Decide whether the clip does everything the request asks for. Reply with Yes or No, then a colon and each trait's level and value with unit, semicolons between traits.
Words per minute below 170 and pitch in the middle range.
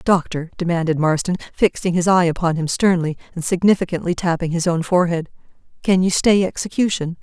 Yes: average, 160 wpm; medium, 175 Hz